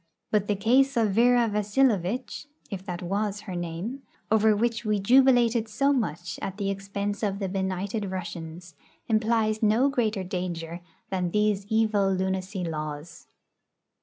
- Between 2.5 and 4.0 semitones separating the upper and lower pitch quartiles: Yes, average, 3.1 semitones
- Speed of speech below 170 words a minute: Yes, average, 140 wpm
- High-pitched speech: Yes, high, 205 Hz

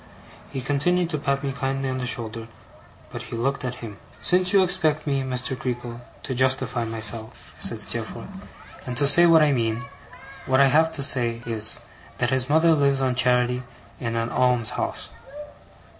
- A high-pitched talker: No, low, 130 Hz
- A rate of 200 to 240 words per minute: No, average, 175 wpm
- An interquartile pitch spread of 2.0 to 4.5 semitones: Yes, average, 2.9 semitones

